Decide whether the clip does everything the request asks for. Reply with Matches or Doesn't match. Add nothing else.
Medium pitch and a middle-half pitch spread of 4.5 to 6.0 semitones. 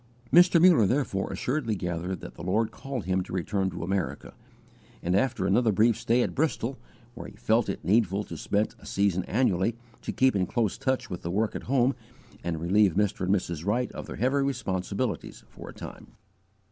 Doesn't match